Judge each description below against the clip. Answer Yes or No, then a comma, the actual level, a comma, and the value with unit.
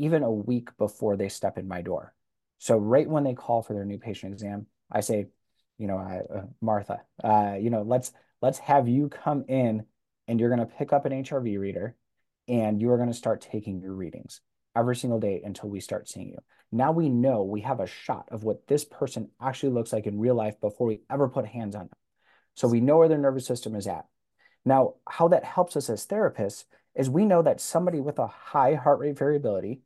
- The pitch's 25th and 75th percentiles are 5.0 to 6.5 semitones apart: No, average, 4.5 semitones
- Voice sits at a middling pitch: No, low, 120 Hz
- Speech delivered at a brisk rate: Yes, fast, 220 wpm